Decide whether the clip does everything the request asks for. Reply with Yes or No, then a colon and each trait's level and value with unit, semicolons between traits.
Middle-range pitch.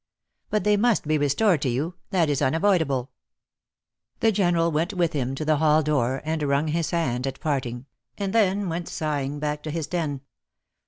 Yes: medium, 155 Hz